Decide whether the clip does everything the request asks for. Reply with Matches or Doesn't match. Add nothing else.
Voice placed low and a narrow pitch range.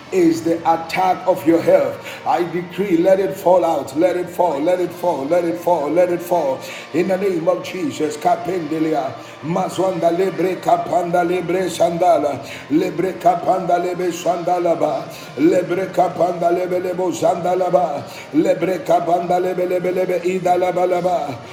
Doesn't match